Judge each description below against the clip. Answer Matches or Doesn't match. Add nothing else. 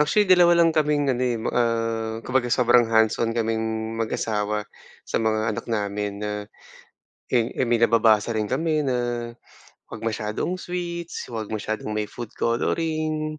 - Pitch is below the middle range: Matches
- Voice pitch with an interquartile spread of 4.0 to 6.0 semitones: Matches